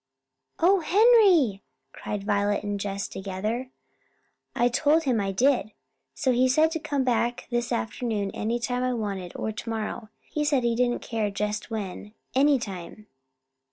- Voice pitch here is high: Yes, high, 235 Hz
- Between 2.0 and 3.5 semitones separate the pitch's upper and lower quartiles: No, average, 4.2 semitones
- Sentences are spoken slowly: No, average, 155 wpm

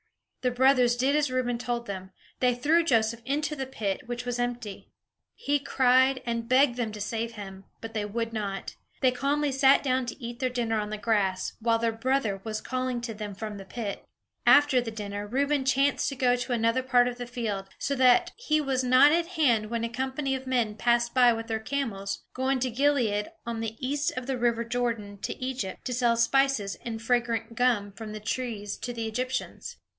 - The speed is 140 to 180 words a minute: No, fast, 205 wpm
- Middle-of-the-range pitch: No, high, 240 Hz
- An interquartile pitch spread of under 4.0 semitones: Yes, average, 2.7 semitones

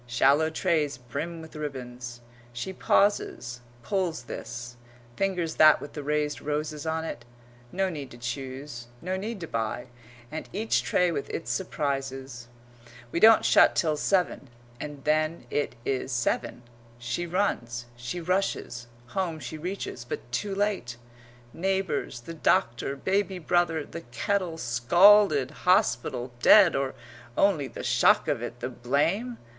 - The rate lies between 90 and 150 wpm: Yes, average, 140 wpm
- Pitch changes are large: Yes, wide, 6.5 semitones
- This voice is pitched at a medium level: Yes, medium, 150 Hz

